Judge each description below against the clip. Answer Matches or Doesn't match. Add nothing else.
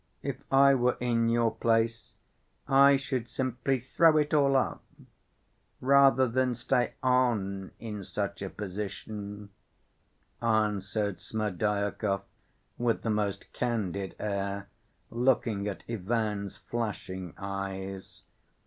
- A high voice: Doesn't match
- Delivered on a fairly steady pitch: Doesn't match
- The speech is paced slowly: Matches